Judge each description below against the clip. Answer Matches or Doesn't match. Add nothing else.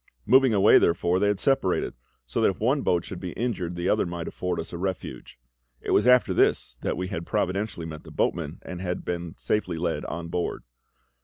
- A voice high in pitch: Doesn't match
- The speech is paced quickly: Matches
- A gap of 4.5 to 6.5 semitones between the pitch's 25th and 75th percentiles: Doesn't match